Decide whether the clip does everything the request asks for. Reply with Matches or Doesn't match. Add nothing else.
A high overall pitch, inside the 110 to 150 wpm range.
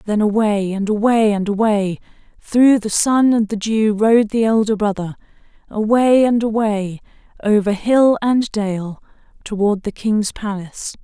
Matches